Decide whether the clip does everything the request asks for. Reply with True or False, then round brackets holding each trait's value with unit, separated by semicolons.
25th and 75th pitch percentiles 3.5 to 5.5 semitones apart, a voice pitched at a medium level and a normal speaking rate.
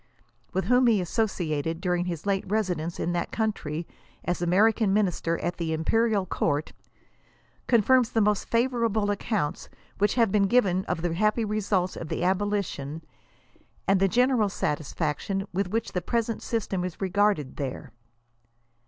False (3.9 semitones; 195 Hz; 150 wpm)